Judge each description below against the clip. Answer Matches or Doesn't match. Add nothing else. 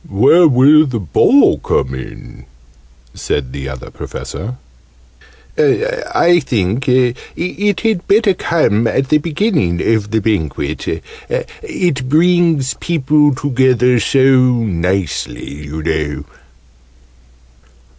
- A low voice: Matches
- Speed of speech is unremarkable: Doesn't match